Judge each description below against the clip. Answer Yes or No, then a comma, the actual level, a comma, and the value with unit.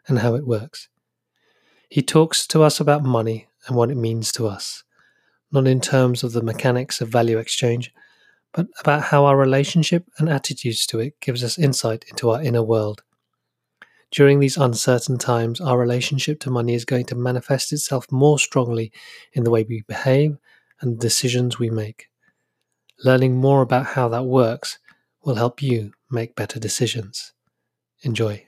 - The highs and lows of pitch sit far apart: No, average, 3.3 semitones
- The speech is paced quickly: No, average, 165 wpm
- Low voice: Yes, low, 125 Hz